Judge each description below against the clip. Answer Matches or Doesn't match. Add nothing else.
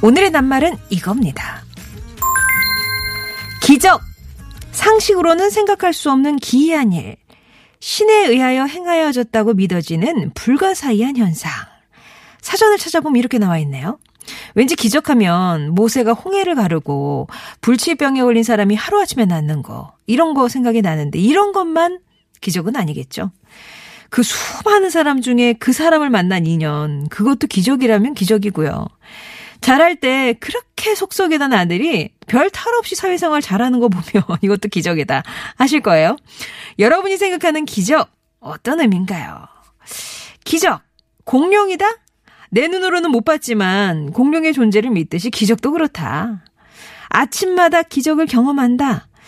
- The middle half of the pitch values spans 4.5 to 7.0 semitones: Doesn't match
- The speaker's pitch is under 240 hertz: Doesn't match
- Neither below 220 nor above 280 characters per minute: Doesn't match